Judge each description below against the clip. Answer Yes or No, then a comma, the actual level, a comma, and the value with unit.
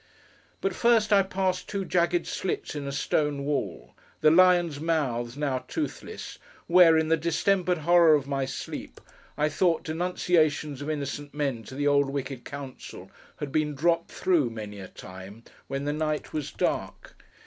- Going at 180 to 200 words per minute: No, average, 155 wpm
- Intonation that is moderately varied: Yes, average, 3.8 semitones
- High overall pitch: No, medium, 150 Hz